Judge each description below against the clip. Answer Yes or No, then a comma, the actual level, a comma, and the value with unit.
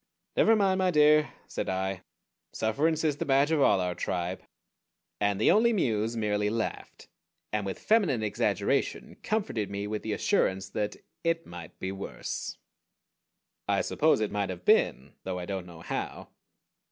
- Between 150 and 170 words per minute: Yes, average, 160 wpm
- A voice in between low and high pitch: No, low, 105 Hz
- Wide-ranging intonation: Yes, wide, 8.0 semitones